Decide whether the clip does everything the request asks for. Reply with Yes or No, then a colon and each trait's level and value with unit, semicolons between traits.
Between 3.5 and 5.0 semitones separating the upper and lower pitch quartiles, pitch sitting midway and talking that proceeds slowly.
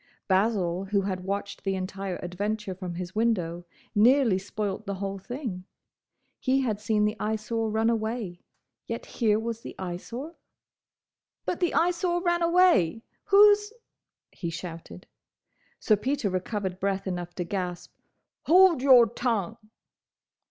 No: average, 4.4 semitones; high, 210 Hz; slow, 130 wpm